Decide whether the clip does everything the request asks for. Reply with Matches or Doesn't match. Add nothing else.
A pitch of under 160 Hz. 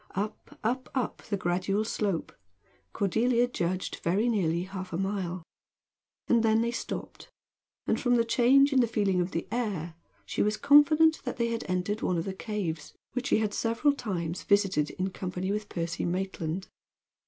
Doesn't match